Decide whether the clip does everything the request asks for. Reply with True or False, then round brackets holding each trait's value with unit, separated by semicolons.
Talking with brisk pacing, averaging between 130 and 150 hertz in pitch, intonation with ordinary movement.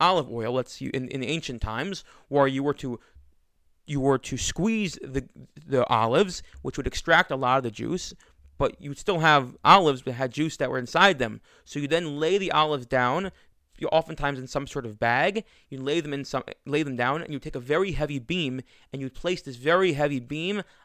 True (220 wpm; 140 Hz; 3.6 semitones)